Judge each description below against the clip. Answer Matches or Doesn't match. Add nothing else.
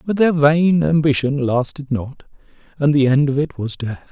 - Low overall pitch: Doesn't match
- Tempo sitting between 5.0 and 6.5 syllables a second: Doesn't match